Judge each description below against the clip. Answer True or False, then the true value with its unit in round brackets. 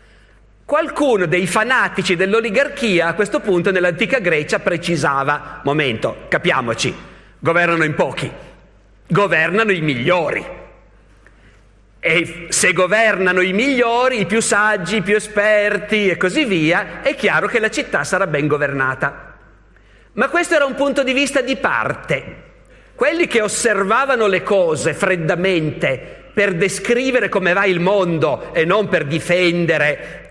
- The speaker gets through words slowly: False (130 wpm)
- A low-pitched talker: False (190 Hz)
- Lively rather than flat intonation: False (4.7 semitones)